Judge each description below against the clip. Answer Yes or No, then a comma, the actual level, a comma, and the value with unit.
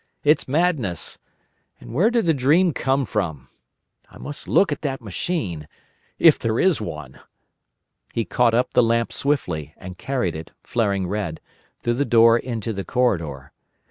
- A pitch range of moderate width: No, wide, 7.4 semitones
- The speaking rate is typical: Yes, average, 155 wpm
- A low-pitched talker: Yes, low, 115 Hz